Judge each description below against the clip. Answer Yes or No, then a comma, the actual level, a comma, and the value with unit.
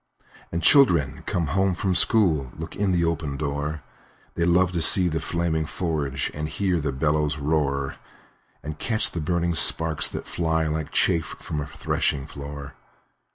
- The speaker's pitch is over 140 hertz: No, very low, 80 Hz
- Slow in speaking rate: No, average, 165 wpm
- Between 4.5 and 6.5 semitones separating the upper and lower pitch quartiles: No, average, 2.7 semitones